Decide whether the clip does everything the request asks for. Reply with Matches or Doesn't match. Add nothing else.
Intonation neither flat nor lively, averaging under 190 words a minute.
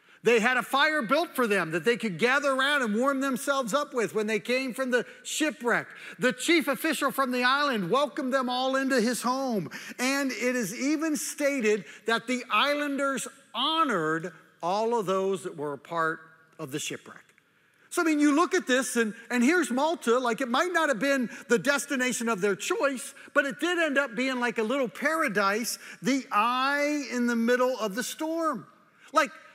Doesn't match